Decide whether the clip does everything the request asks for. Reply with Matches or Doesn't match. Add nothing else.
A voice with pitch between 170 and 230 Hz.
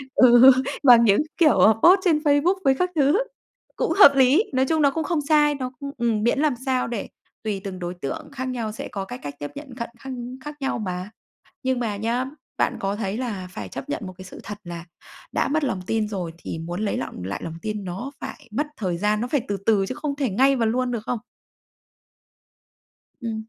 Doesn't match